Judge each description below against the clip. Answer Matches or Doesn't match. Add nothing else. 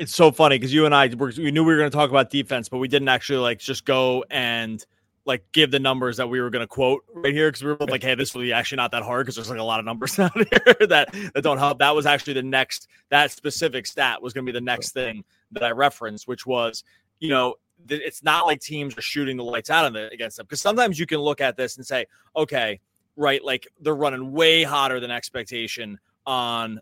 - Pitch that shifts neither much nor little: Matches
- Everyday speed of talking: Doesn't match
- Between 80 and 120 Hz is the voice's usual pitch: Doesn't match